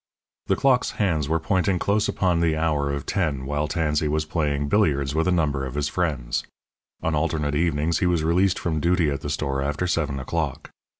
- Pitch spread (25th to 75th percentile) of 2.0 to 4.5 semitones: Yes, average, 2.9 semitones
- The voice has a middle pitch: No, very low, 80 Hz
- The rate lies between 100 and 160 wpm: No, average, 195 wpm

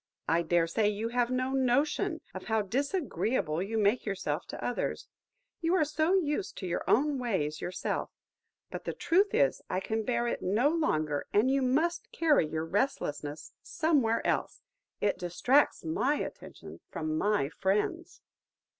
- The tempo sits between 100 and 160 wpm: Yes, average, 155 wpm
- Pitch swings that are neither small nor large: No, wide, 8.4 semitones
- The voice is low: No, high, 230 Hz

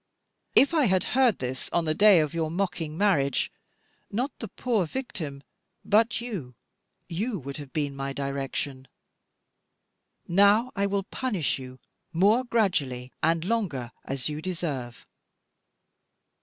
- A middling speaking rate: No, slow, 130 wpm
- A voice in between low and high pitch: Yes, medium, 170 Hz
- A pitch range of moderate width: No, wide, 7.1 semitones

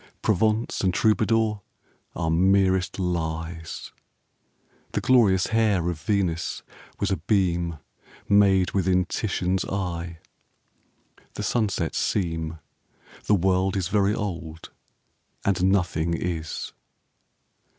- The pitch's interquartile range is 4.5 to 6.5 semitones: No, average, 3.1 semitones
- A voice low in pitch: Yes, very low, 95 Hz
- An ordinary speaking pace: No, slow, 100 wpm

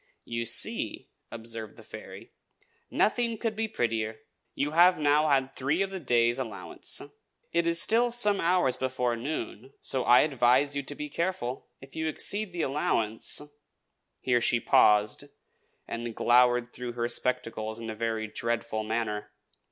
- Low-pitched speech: Yes, low, 125 Hz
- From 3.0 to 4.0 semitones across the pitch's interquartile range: No, average, 5.3 semitones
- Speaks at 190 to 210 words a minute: No, average, 155 wpm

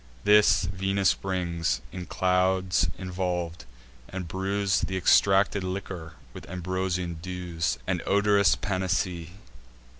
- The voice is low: Yes, very low, 90 Hz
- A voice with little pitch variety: Yes, narrow, 1.8 semitones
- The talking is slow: Yes, slow, 100 wpm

